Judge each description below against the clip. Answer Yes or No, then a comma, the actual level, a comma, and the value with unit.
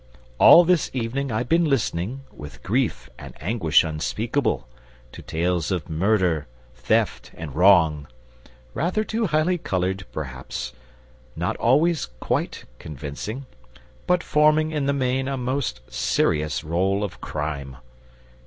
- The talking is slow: Yes, slow, 125 wpm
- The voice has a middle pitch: No, low, 100 Hz